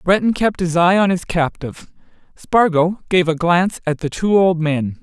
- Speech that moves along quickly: No, average, 190 wpm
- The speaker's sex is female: No, male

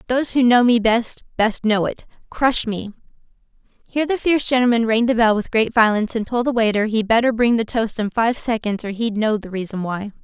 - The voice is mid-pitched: No, high, 225 Hz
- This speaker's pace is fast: Yes, fast, 225 wpm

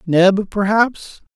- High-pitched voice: Yes, high, 200 Hz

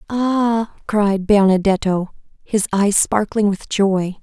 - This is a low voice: No, high, 205 Hz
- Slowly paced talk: Yes, slow, 115 wpm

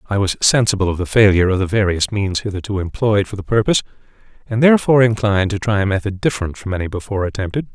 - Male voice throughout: Yes, male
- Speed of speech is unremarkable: No, fast, 210 wpm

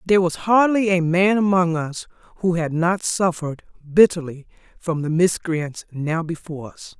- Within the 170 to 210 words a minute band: No, average, 155 wpm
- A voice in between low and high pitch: Yes, medium, 170 Hz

